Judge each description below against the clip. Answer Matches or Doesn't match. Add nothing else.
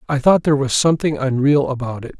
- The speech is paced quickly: Matches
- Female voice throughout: Doesn't match